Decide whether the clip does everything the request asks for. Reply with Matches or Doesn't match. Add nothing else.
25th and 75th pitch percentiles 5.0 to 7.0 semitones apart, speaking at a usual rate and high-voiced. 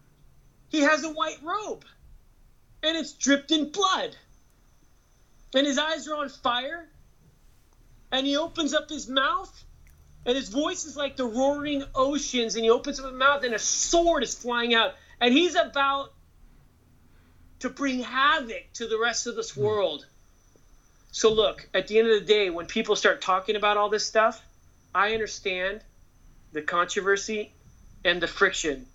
Matches